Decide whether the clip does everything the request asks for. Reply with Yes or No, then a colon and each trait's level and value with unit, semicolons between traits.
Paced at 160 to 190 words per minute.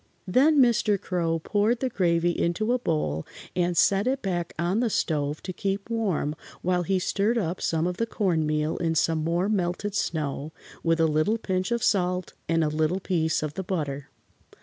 Yes: average, 185 wpm